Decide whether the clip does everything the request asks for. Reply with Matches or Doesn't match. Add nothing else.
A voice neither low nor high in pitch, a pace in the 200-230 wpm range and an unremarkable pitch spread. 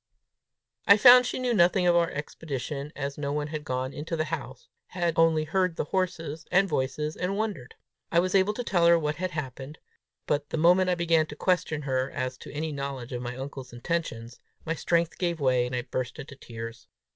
Matches